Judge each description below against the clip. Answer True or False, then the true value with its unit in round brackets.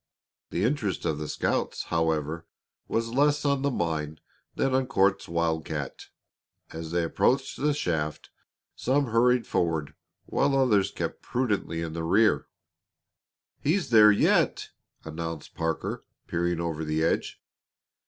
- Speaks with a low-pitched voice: True (85 Hz)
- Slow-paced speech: True (130 wpm)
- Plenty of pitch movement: True (7.7 semitones)